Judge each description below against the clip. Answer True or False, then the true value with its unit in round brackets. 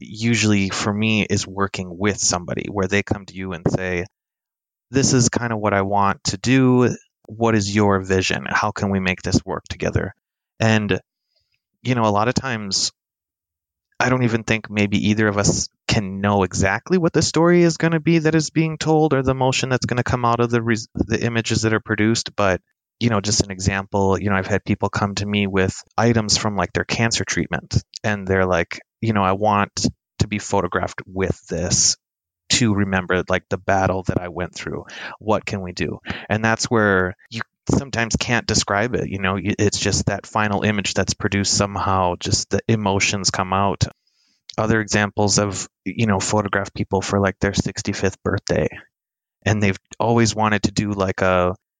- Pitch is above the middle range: False (100 Hz)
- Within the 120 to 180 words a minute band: False (195 wpm)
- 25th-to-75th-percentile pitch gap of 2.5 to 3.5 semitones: True (2.8 semitones)